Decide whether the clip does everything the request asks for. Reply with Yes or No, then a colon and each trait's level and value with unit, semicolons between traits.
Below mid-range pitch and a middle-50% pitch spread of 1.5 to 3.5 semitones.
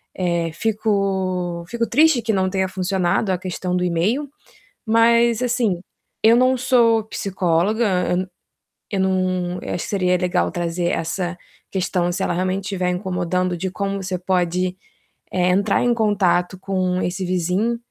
No: medium, 185 Hz; average, 2.9 semitones